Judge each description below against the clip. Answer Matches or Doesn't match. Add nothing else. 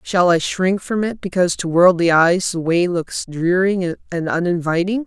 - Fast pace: Doesn't match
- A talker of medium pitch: Matches